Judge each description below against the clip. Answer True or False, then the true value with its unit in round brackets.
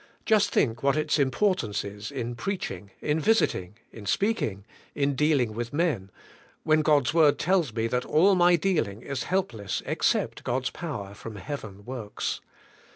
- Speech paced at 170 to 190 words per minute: False (155 wpm)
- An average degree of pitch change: False (6.9 semitones)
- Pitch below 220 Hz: True (135 Hz)